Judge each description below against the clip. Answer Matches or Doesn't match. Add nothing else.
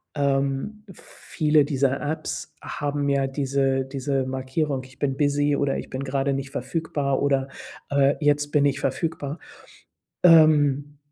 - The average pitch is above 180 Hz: Doesn't match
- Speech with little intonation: Matches